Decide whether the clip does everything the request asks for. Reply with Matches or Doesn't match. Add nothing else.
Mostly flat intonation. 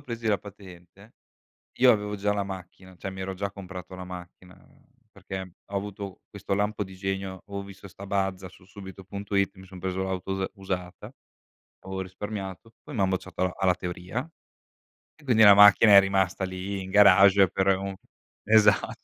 Matches